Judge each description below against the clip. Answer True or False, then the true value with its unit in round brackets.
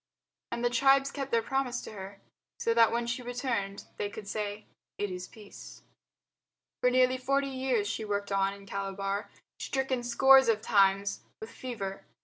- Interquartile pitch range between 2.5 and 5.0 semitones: True (4.2 semitones)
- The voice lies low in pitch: False (230 Hz)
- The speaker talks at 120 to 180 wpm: True (165 wpm)